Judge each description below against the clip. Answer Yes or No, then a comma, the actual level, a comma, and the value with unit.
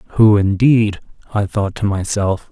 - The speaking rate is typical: Yes, average, 145 wpm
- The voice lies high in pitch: No, low, 100 Hz